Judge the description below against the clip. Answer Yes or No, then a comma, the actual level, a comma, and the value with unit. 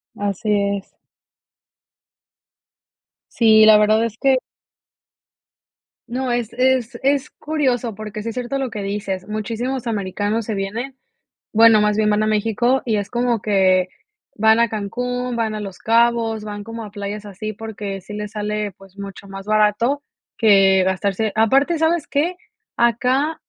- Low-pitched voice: No, high, 220 Hz